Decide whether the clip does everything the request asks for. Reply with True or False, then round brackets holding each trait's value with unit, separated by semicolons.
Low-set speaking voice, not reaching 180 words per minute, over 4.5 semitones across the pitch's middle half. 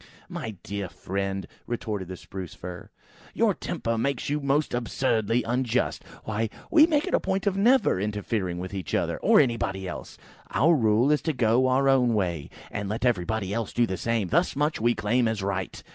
False (115 Hz; 190 wpm; 5.1 semitones)